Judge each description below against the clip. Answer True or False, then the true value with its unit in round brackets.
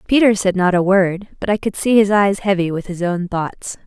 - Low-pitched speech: False (195 Hz)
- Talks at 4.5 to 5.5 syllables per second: True (5.1 syllables/s)